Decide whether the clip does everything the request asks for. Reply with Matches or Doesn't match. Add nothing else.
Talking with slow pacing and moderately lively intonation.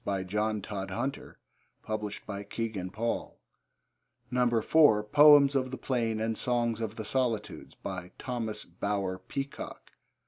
Matches